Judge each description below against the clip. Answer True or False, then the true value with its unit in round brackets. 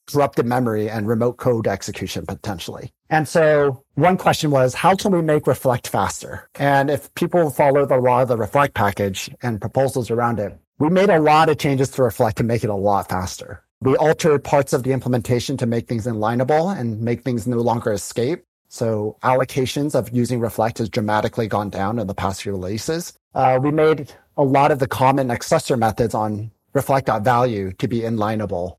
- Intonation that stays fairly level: False (4.5 semitones)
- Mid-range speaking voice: False (125 Hz)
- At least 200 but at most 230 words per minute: False (190 wpm)